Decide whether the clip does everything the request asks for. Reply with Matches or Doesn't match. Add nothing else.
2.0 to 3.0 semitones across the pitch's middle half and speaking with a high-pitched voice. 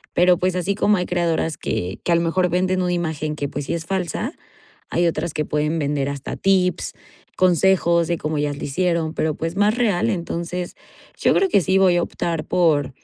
Doesn't match